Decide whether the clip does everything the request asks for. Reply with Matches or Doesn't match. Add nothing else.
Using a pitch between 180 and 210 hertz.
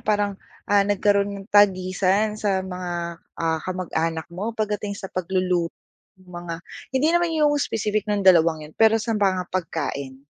Matches